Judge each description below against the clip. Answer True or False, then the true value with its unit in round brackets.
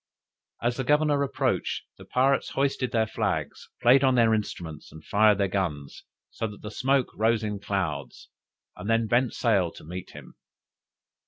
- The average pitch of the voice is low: True (110 Hz)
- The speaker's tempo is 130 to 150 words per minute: False (165 wpm)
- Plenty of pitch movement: False (4.5 semitones)